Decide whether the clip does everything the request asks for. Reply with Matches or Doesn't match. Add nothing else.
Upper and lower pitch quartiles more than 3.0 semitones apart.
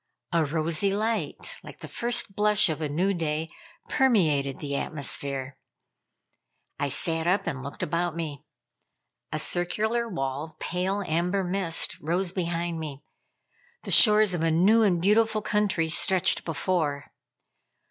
Matches